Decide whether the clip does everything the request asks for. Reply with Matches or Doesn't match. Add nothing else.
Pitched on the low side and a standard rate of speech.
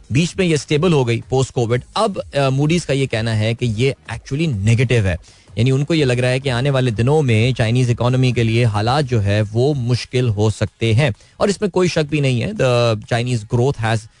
Doesn't match